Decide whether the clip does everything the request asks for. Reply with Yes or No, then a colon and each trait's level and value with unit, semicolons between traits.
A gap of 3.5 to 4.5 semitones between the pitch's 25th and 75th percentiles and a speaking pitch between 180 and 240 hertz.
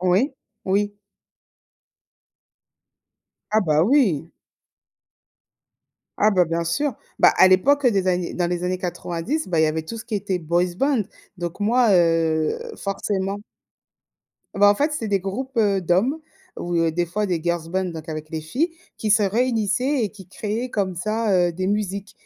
Yes: average, 4.0 semitones; high, 190 Hz